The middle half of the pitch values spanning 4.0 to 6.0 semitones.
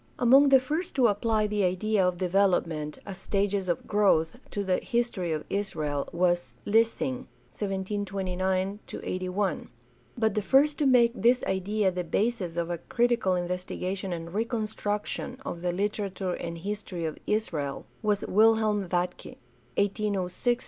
No: average, 3.2 semitones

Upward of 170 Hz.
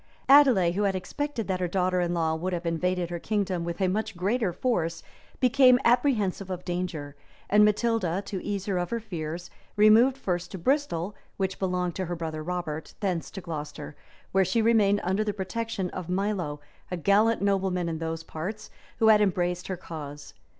Yes: medium, 185 Hz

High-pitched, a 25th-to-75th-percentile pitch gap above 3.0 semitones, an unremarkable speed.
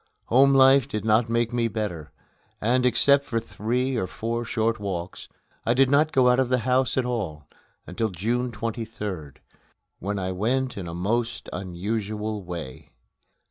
No: low, 115 Hz; average, 4.0 semitones; average, 160 wpm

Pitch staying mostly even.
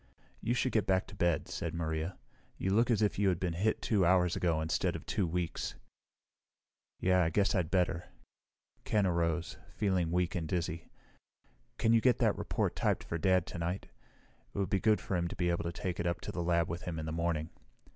Yes: narrow, 2.3 semitones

